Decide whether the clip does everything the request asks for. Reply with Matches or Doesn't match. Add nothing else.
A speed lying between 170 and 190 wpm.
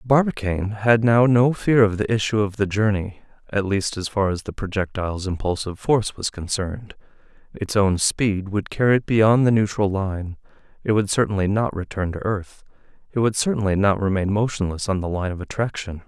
Matches